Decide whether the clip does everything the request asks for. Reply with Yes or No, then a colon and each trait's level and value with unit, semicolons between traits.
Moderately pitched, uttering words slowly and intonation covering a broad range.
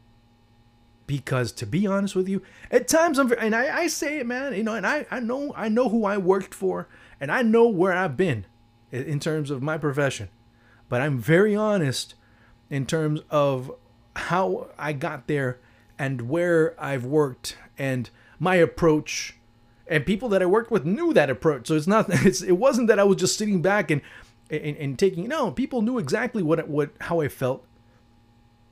No: medium, 155 Hz; average, 190 wpm; wide, 8.5 semitones